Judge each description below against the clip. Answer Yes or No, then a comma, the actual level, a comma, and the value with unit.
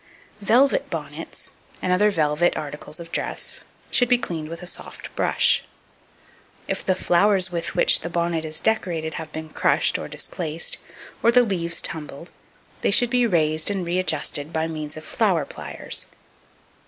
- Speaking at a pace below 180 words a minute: Yes, average, 155 wpm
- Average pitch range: Yes, average, 3.7 semitones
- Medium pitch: Yes, medium, 170 Hz